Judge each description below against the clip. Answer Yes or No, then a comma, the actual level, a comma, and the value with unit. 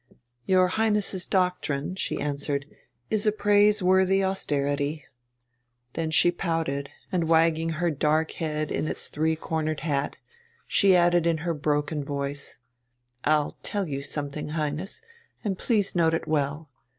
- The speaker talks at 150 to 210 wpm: No, slow, 135 wpm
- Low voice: No, medium, 160 Hz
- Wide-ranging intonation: No, average, 3.8 semitones